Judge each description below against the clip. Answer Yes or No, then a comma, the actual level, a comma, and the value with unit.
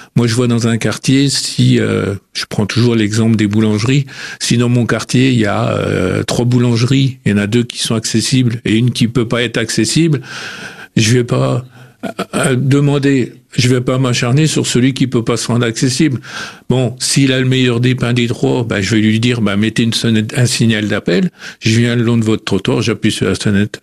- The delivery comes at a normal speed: No, fast, 225 wpm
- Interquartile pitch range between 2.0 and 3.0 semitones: Yes, narrow, 2.6 semitones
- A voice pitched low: Yes, low, 120 Hz